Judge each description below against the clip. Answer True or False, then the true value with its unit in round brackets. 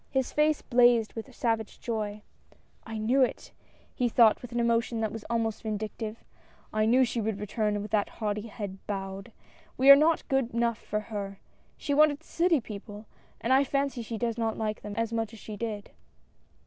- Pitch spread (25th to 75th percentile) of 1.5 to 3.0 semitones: True (2.5 semitones)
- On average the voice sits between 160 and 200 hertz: False (225 Hz)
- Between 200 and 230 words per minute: True (205 wpm)